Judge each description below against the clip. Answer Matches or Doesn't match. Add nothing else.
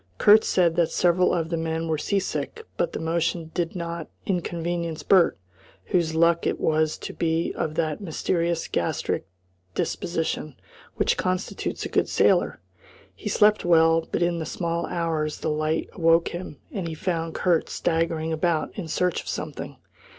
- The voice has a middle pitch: Matches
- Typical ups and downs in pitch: Doesn't match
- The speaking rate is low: Doesn't match